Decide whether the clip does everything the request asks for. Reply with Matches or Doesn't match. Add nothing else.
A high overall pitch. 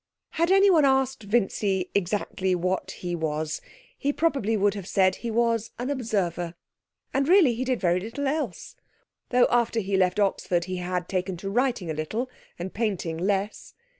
Matches